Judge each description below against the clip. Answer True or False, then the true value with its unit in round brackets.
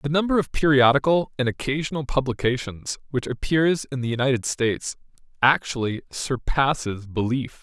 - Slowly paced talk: True (125 wpm)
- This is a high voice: False (135 Hz)